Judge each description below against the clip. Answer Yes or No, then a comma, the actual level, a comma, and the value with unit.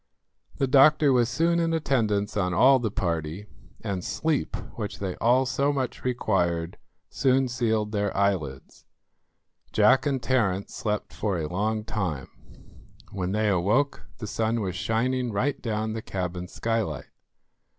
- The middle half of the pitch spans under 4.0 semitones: No, average, 5.1 semitones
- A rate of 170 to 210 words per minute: No, average, 140 wpm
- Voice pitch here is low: Yes, low, 110 Hz